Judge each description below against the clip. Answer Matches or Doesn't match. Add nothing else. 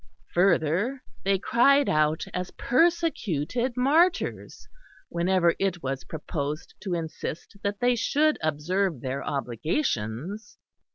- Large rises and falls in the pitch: Matches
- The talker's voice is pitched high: Doesn't match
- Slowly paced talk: Matches